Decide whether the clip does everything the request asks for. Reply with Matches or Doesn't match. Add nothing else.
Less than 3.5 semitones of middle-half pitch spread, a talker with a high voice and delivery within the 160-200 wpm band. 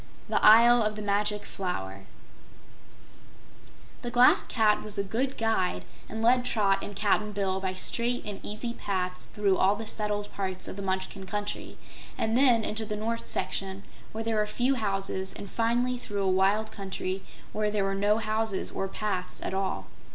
Matches